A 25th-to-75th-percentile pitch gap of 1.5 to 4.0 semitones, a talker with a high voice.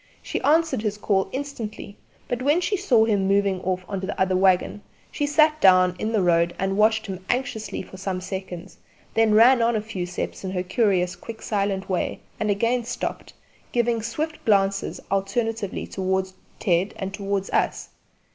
Yes: average, 3.4 semitones; high, 200 Hz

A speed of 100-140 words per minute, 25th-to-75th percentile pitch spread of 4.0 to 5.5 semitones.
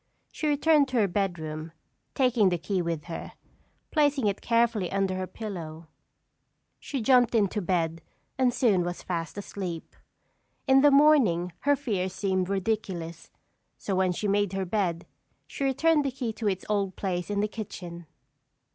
No: average, 155 wpm; average, 5.2 semitones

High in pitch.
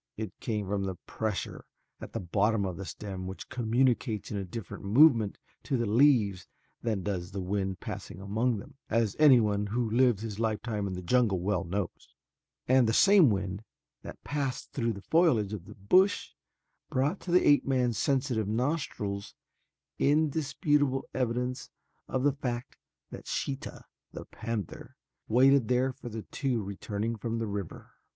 No: low, 115 Hz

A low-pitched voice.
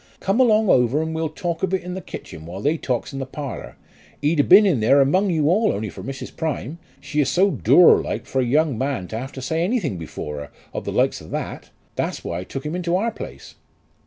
No: medium, 150 Hz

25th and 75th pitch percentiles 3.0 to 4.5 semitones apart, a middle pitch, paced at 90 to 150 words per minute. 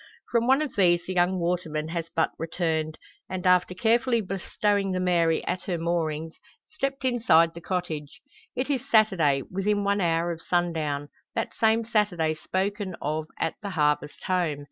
No: average, 4.0 semitones; medium, 180 Hz; average, 165 wpm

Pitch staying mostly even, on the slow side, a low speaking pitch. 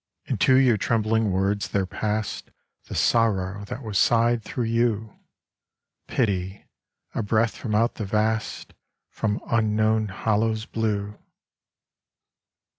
Yes: narrow, 1.8 semitones; slow, 115 wpm; low, 110 Hz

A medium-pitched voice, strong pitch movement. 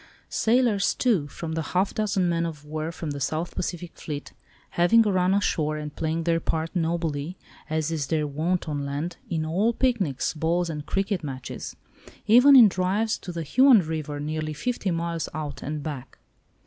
No: medium, 165 Hz; average, 3.7 semitones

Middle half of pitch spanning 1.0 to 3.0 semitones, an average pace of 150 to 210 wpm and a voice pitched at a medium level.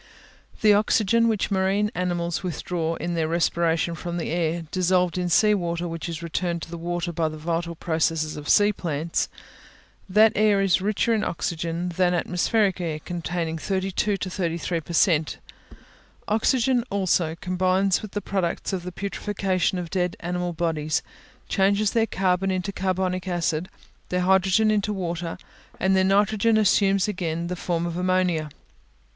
Yes: narrow, 2.6 semitones; average, 155 wpm; medium, 180 Hz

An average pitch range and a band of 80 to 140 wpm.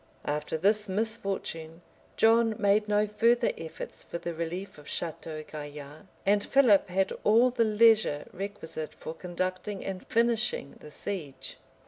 Yes: average, 5.0 semitones; slow, 135 wpm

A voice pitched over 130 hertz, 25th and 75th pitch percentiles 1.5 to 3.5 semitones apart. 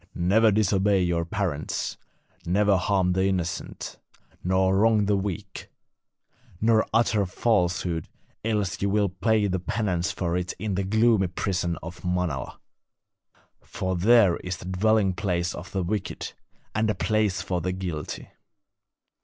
No: very low, 95 Hz; average, 2.8 semitones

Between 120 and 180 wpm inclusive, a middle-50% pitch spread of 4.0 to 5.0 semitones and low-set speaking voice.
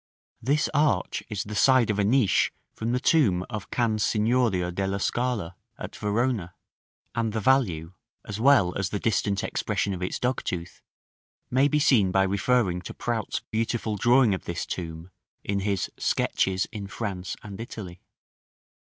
Yes: average, 155 wpm; average, 4.3 semitones; low, 105 Hz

